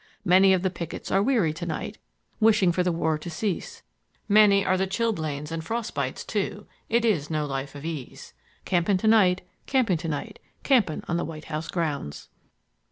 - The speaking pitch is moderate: Yes, medium, 180 Hz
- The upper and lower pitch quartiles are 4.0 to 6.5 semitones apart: Yes, average, 4.5 semitones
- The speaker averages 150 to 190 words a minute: Yes, average, 185 wpm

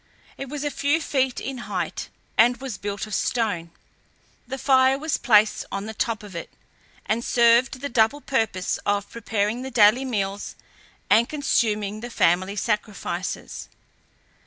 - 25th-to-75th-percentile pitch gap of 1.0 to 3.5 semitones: No, average, 4.3 semitones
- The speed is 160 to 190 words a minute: No, average, 150 wpm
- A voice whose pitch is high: Yes, high, 225 Hz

